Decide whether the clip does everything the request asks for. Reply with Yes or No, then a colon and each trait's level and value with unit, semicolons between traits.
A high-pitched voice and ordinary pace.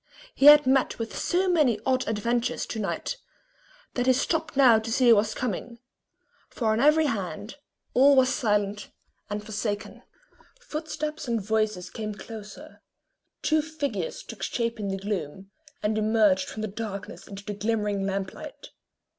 Yes: high, 220 Hz; average, 160 wpm